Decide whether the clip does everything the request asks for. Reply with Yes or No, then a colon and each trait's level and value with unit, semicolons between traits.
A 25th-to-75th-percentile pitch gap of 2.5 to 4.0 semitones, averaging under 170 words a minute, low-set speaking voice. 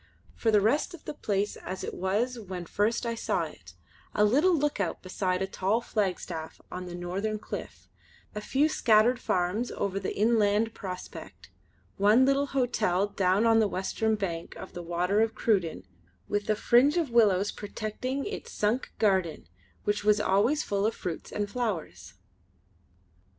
No: average, 3.7 semitones; average, 160 wpm; high, 210 Hz